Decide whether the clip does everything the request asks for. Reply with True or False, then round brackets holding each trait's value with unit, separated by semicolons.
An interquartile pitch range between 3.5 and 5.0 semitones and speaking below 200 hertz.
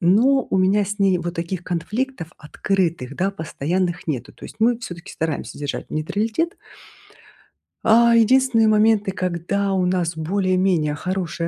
True (4.0 semitones; 185 Hz)